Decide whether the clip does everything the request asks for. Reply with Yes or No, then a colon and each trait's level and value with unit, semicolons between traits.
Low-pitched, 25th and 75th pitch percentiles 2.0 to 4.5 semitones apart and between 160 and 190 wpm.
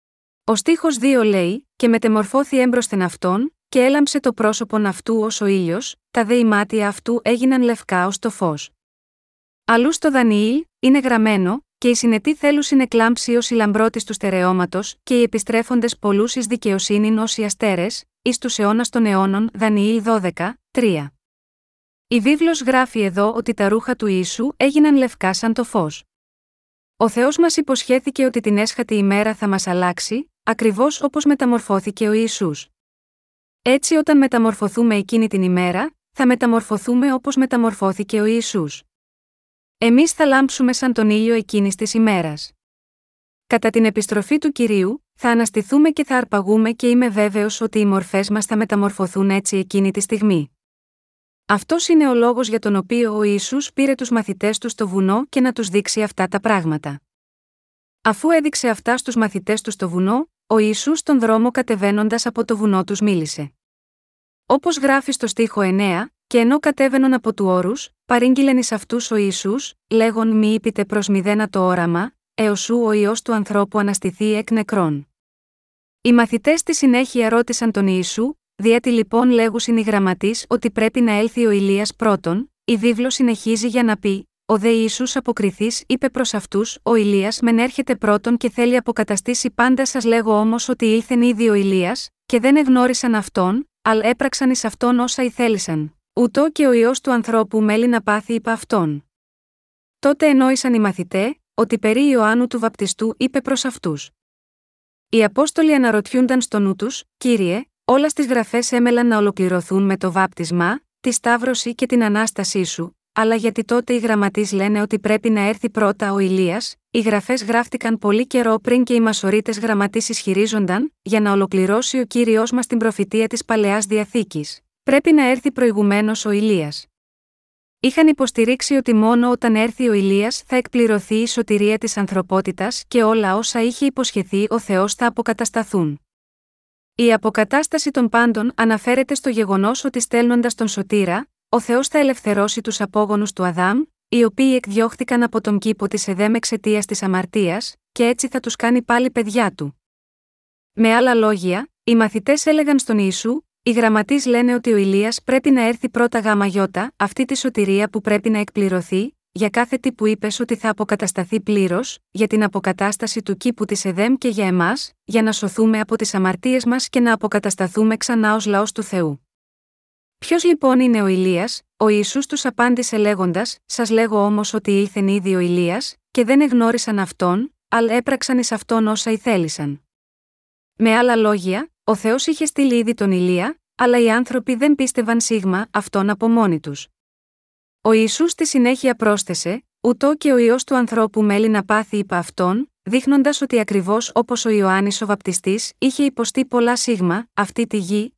No: high, 225 Hz; average, 3.2 semitones; average, 165 wpm